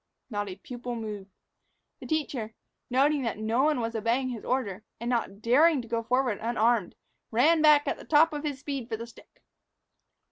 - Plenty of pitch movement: No, average, 4.0 semitones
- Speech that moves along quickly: No, average, 185 wpm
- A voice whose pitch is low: No, high, 240 Hz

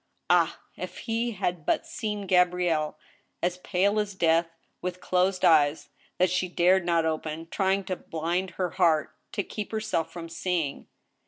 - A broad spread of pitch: No, narrow, 2.5 semitones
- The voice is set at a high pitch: No, medium, 180 Hz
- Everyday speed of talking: Yes, average, 160 wpm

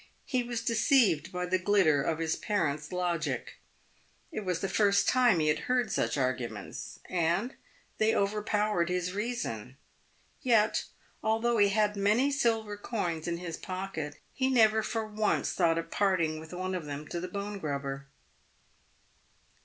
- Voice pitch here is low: No, high, 195 Hz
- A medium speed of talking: Yes, average, 155 wpm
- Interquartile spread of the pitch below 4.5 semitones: No, average, 4.8 semitones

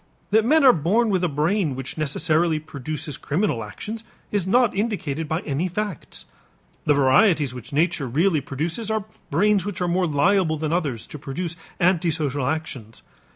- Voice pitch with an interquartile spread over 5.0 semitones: Yes, wide, 5.5 semitones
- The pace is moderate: Yes, average, 160 wpm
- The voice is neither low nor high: Yes, medium, 160 Hz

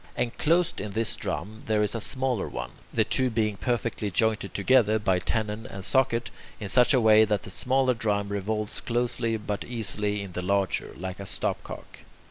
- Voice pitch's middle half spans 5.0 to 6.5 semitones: No, average, 2.8 semitones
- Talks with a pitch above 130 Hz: No, low, 110 Hz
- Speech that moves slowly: No, average, 180 wpm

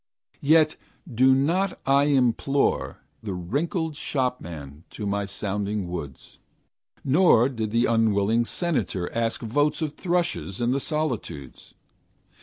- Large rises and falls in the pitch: Yes, wide, 6.4 semitones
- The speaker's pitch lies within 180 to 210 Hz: No, low, 120 Hz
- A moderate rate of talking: No, slow, 115 wpm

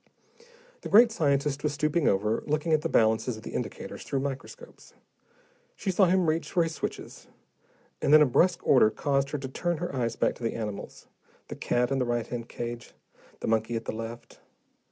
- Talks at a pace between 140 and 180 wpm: No, average, 195 wpm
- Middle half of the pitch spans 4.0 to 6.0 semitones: Yes, average, 5.1 semitones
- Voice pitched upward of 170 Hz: No, low, 135 Hz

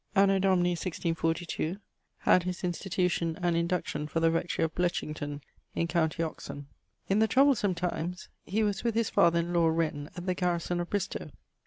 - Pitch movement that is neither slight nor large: No, narrow, 2.2 semitones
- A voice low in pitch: No, medium, 175 Hz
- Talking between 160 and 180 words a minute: Yes, average, 170 wpm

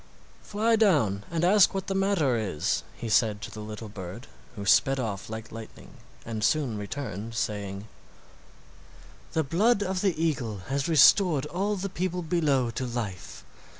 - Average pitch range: No, wide, 8.9 semitones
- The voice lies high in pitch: No, low, 135 Hz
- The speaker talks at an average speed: Yes, average, 155 wpm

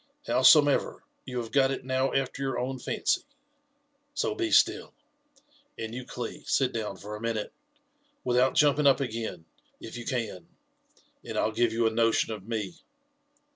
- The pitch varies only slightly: No, average, 3.2 semitones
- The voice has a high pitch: No, low, 125 Hz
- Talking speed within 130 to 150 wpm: No, average, 160 wpm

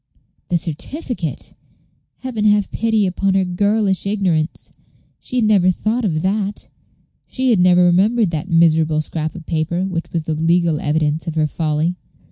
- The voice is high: No, medium, 180 Hz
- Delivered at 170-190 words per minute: No, average, 155 wpm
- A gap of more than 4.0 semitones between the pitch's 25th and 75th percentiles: Yes, average, 4.4 semitones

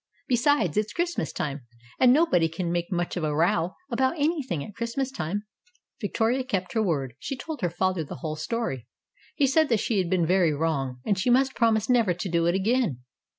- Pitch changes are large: Yes, wide, 6.9 semitones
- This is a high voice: Yes, high, 195 Hz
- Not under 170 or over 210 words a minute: Yes, average, 200 wpm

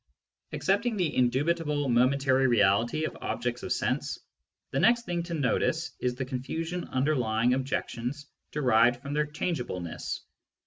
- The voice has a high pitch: No, low, 135 Hz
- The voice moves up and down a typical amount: Yes, average, 4.4 semitones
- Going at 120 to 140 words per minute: Yes, slow, 135 wpm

